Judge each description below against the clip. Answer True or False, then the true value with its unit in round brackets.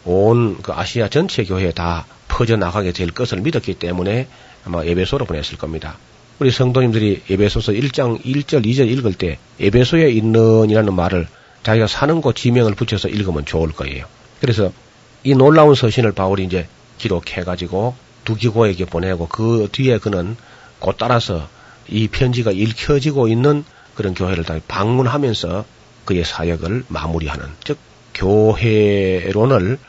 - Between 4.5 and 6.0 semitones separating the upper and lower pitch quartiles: True (5.3 semitones)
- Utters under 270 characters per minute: False (320 characters per minute)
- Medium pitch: False (110 Hz)